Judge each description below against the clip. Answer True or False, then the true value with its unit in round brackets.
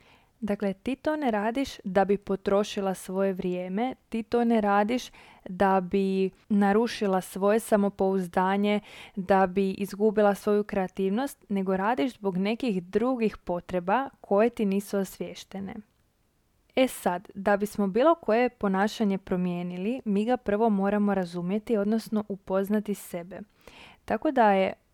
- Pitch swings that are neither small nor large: False (2.2 semitones)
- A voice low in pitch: False (205 Hz)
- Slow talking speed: False (130 wpm)